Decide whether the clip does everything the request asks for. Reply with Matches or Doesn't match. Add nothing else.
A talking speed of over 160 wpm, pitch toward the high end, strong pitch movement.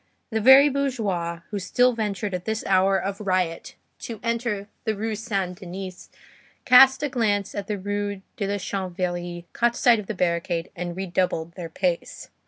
Doesn't match